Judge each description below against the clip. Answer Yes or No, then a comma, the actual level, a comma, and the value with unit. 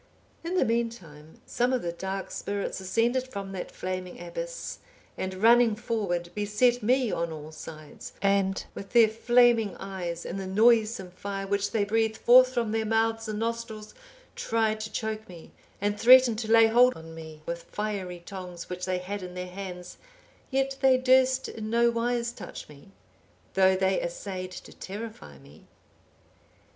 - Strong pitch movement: No, average, 4.0 semitones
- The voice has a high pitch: Yes, high, 210 Hz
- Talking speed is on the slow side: No, average, 165 wpm